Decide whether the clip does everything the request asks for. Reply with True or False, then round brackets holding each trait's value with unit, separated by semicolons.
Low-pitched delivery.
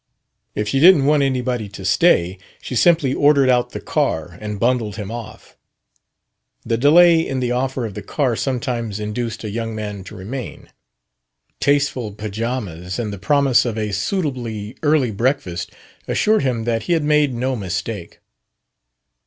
True (120 Hz)